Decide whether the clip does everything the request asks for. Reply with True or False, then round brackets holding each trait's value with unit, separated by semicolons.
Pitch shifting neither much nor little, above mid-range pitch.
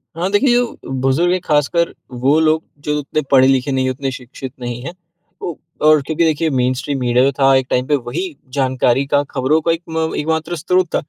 False (3.6 semitones; 140 Hz)